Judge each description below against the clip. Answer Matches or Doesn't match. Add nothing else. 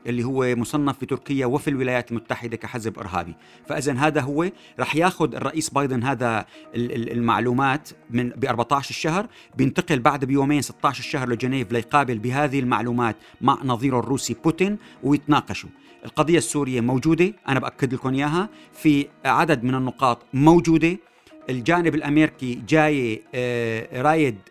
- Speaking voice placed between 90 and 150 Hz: Matches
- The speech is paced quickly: Doesn't match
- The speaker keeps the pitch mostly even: Doesn't match